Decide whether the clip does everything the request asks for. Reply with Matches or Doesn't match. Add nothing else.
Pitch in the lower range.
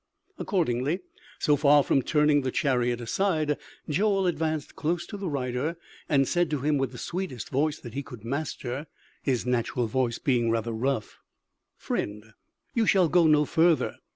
Doesn't match